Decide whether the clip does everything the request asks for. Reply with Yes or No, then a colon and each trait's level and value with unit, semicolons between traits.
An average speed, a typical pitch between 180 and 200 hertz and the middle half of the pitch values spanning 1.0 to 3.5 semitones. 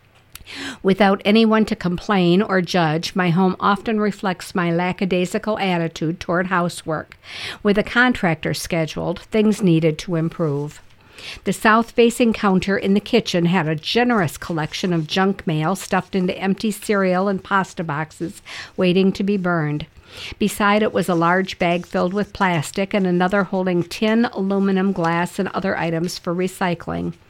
Yes: average, 150 wpm; medium, 185 Hz; average, 2.8 semitones